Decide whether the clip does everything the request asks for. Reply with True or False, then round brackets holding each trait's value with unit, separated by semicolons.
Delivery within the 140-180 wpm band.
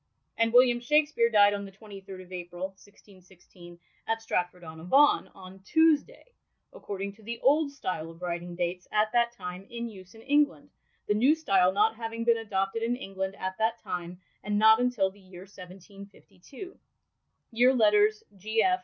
True (165 wpm)